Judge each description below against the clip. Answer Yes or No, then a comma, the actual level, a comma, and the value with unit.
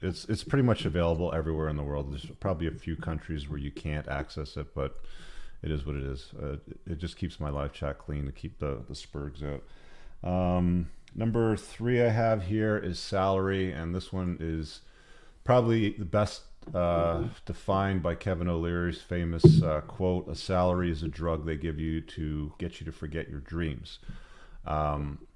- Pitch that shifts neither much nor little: Yes, average, 3.8 semitones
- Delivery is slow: No, average, 185 wpm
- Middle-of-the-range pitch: No, very low, 85 Hz